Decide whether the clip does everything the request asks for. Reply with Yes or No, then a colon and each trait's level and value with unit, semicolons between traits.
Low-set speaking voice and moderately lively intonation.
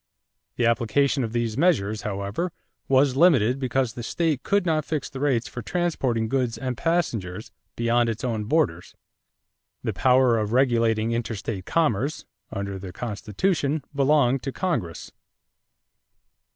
Yes: low, 125 Hz; average, 4.3 semitones